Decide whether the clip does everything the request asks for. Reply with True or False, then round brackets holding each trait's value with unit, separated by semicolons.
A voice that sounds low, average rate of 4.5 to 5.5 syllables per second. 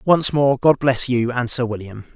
True (125 Hz; 4.7 syllables/s)